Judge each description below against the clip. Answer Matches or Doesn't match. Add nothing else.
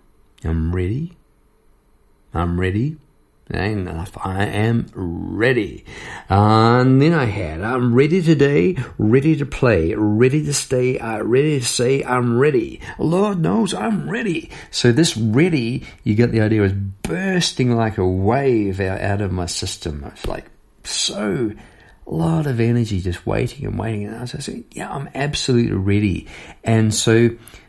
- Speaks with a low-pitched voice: Matches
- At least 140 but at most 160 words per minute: Matches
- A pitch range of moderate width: Doesn't match